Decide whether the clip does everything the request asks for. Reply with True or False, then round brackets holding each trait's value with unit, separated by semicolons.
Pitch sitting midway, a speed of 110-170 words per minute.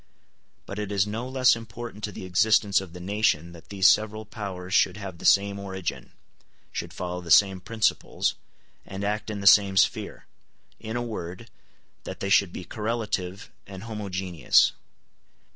False (100 Hz; 160 wpm)